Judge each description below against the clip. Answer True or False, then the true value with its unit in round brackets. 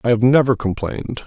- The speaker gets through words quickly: False (190 wpm)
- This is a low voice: True (120 Hz)